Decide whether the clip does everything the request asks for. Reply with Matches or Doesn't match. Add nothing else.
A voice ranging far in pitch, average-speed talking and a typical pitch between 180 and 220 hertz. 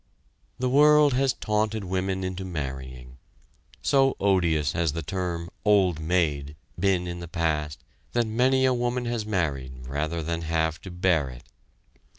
Doesn't match